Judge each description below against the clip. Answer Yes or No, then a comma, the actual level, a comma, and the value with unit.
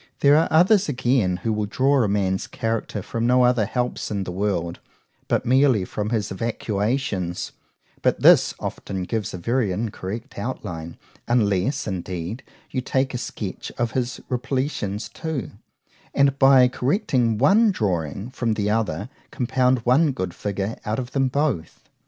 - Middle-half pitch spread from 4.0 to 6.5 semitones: Yes, average, 4.6 semitones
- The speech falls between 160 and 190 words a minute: No, average, 145 wpm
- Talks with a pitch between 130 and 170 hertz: No, low, 115 Hz